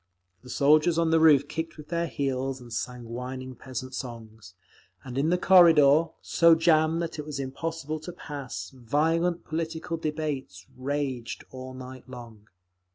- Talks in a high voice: No, medium, 140 Hz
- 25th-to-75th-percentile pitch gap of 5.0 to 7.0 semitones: No, average, 4.0 semitones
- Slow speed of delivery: No, average, 155 wpm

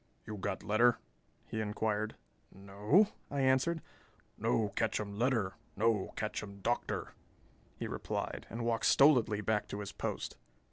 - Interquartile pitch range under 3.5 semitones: Yes, average, 2.7 semitones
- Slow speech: Yes, slow, 130 wpm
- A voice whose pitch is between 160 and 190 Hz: No, low, 110 Hz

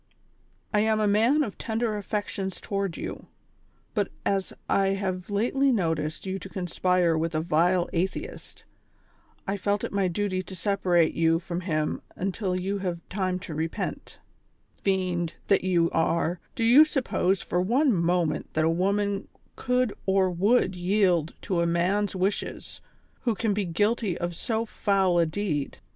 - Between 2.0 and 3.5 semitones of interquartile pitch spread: Yes, average, 3.0 semitones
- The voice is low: No, high, 190 Hz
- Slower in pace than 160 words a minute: No, average, 165 wpm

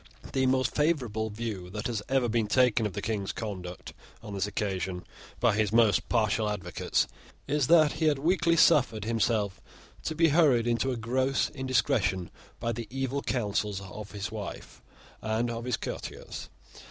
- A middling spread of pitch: Yes, average, 4.1 semitones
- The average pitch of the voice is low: Yes, low, 115 Hz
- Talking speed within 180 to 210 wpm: No, average, 165 wpm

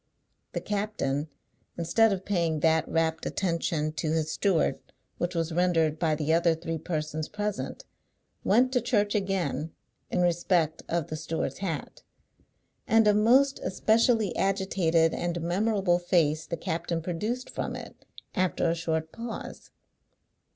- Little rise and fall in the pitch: No, average, 3.9 semitones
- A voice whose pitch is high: No, medium, 170 Hz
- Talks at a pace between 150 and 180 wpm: No, slow, 135 wpm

